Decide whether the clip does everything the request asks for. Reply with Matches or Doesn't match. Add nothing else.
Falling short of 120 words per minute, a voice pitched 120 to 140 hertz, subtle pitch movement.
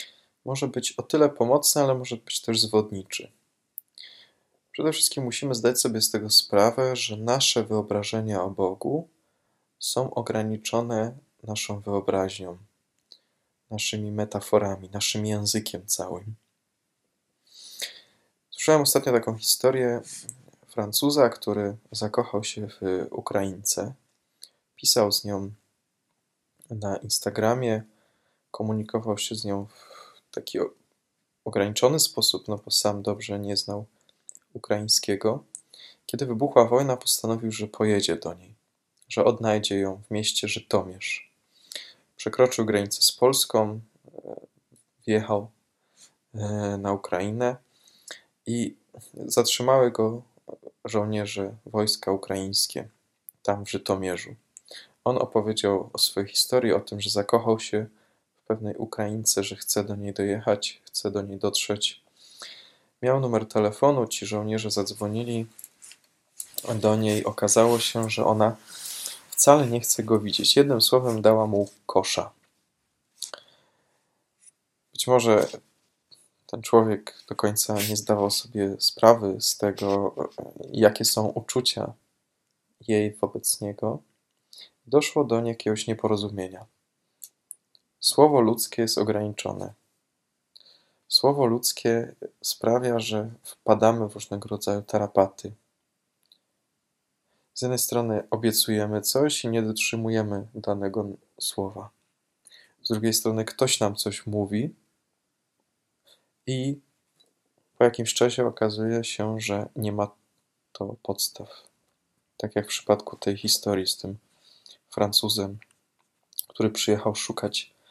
Doesn't match